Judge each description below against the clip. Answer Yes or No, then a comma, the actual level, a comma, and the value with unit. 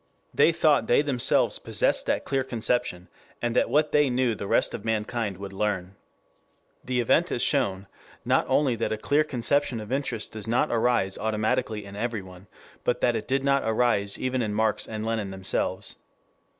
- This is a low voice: Yes, low, 115 Hz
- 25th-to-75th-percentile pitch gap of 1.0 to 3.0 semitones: No, average, 3.7 semitones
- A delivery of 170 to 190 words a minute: Yes, average, 175 wpm